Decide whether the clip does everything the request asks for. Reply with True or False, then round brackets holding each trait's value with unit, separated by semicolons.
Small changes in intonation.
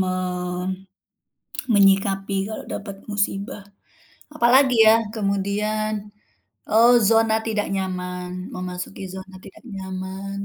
True (2.2 semitones)